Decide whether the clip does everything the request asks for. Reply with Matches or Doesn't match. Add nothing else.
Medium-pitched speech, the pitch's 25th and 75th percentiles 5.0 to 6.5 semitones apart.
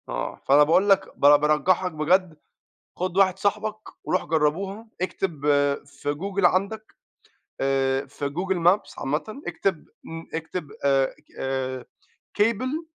Matches